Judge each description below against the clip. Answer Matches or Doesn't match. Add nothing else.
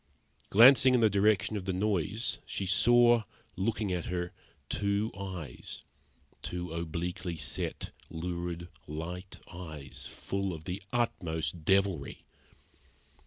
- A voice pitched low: Matches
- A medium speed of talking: Doesn't match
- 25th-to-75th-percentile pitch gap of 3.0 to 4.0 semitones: Matches